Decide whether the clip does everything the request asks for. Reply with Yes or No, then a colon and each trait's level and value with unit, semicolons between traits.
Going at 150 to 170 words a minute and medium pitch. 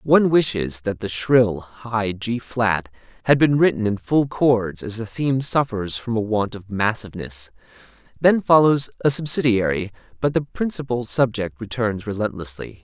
No: average, 155 wpm; low, 115 Hz